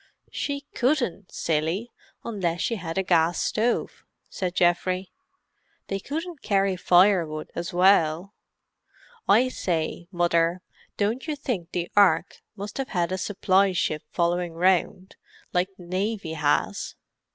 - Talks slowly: Yes, slow, 130 wpm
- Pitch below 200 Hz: Yes, medium, 185 Hz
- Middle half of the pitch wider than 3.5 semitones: No, average, 3.1 semitones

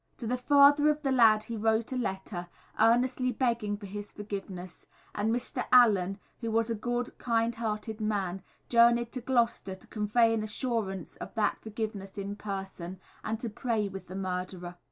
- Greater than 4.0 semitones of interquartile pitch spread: No, average, 3.2 semitones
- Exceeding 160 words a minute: Yes, average, 175 wpm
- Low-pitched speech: No, high, 220 Hz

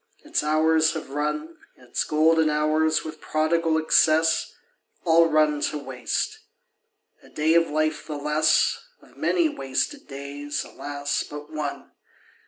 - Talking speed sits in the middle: No, slow, 130 wpm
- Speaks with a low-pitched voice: No, medium, 155 Hz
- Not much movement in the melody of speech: Yes, narrow, 1.5 semitones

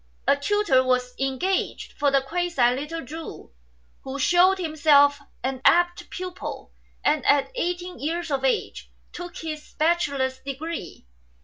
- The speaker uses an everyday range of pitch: Yes, average, 4.6 semitones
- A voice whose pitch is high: Yes, very high, 300 Hz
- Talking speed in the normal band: No, slow, 130 wpm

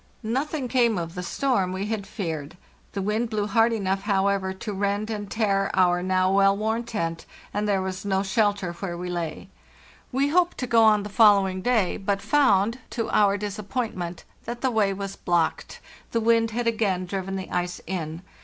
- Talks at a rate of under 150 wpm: No, average, 190 wpm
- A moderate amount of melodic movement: Yes, average, 3.1 semitones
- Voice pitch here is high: Yes, high, 200 Hz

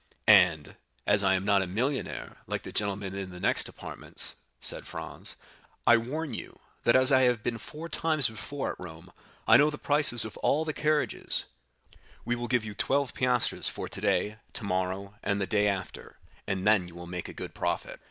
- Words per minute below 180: No, average, 190 wpm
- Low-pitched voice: Yes, low, 105 Hz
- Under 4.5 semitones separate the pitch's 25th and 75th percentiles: No, average, 5.3 semitones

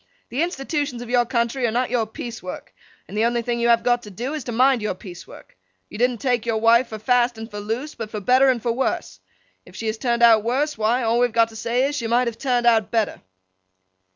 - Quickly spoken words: Yes, fast, 250 wpm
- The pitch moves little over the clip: Yes, narrow, 2.0 semitones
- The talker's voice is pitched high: Yes, high, 235 Hz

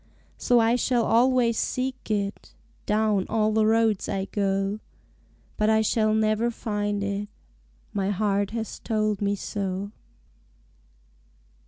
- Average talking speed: No, slow, 125 wpm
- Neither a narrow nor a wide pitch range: No, narrow, 1.9 semitones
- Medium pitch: No, high, 215 Hz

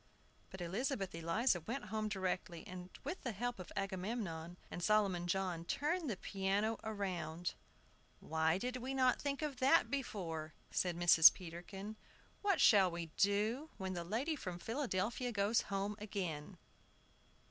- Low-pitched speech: No, high, 195 Hz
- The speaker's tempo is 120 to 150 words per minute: Yes, average, 145 wpm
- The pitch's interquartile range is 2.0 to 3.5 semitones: No, average, 5.2 semitones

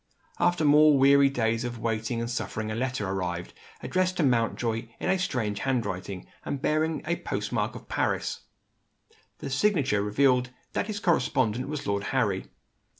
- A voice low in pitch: Yes, low, 125 Hz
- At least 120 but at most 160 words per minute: Yes, average, 155 wpm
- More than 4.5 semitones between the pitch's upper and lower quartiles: Yes, average, 4.9 semitones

